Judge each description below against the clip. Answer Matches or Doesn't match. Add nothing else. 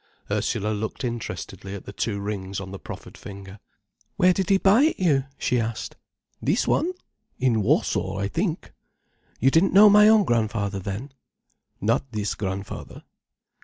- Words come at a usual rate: Matches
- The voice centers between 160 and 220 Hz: Doesn't match